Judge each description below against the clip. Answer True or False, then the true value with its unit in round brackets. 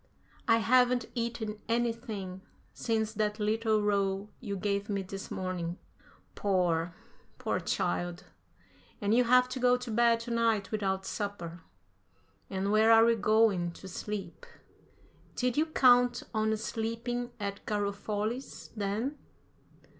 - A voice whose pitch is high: True (215 Hz)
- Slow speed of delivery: True (125 wpm)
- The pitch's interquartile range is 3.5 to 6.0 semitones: False (2.8 semitones)